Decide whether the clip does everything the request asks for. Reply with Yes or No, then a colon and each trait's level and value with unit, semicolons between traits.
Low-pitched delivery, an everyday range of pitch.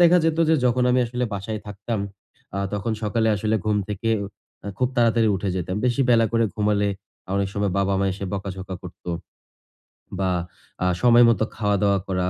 Yes: low, 105 Hz; average, 3.1 semitones